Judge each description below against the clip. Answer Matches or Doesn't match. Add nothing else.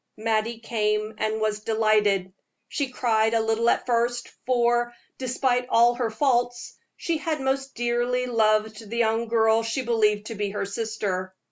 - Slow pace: Doesn't match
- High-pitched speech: Matches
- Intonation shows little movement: Matches